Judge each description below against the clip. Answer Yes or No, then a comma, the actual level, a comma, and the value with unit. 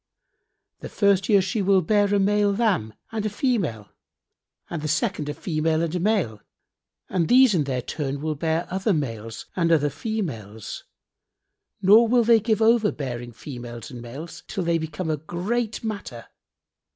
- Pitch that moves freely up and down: Yes, wide, 6.7 semitones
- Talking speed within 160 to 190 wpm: Yes, average, 165 wpm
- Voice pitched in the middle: Yes, medium, 170 Hz